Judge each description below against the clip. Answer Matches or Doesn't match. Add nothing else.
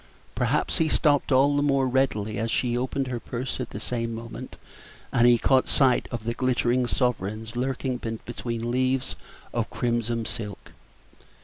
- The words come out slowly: Doesn't match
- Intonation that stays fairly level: Matches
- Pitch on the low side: Matches